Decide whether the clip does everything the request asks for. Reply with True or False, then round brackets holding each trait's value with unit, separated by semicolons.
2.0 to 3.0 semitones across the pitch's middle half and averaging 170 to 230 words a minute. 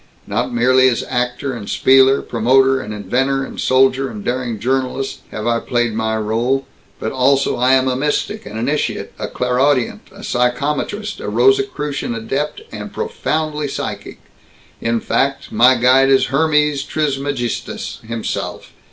False (2.6 semitones; 145 wpm)